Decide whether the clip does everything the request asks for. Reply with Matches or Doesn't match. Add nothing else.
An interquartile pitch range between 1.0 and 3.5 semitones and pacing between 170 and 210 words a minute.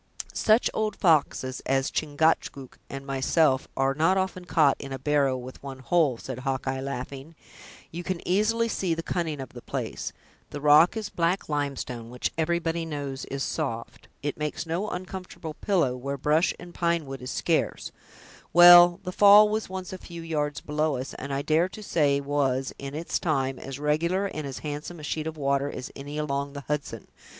Doesn't match